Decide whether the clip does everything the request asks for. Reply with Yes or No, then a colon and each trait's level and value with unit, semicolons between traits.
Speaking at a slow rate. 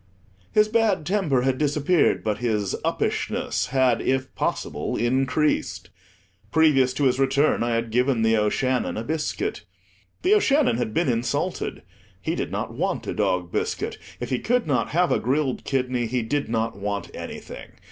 No: average, 160 wpm